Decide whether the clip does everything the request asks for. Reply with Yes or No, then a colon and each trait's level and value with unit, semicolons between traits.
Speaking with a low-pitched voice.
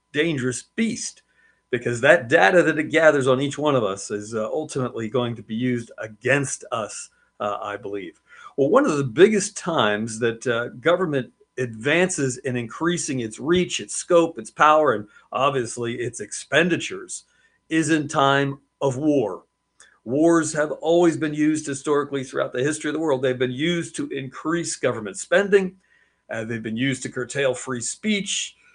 No: medium, 145 Hz